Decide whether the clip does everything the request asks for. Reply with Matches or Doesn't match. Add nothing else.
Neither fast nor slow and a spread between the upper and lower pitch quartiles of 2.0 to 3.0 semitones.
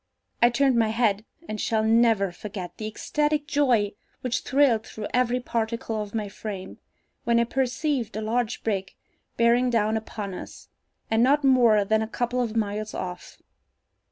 Matches